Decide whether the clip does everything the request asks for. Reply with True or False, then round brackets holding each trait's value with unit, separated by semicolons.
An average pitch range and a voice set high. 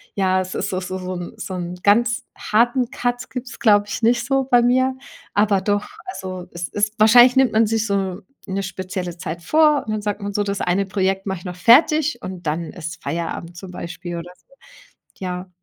True (4.6 semitones; 200 Hz)